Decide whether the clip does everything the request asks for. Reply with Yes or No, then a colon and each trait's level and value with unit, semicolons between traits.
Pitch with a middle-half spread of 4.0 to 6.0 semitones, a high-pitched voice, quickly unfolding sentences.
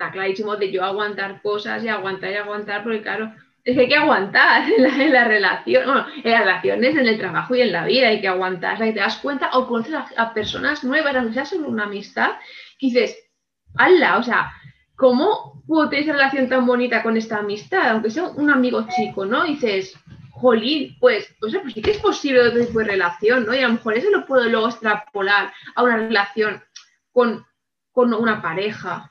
Yes: average, 4.5 semitones; high, 230 Hz; fast, 215 wpm